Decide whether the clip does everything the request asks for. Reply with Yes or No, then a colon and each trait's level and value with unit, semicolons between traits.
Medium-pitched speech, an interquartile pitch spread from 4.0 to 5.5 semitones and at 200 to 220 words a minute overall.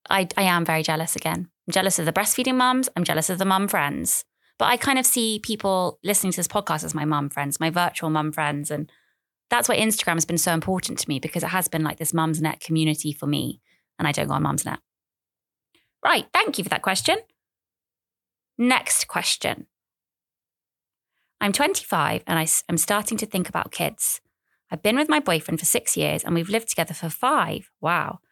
Yes: medium, 175 Hz; average, 4.7 semitones; fast, 205 wpm